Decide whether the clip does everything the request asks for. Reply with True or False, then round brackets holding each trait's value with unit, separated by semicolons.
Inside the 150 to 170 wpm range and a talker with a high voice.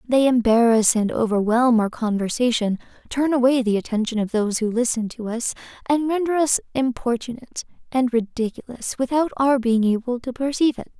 True (160 wpm; 240 Hz)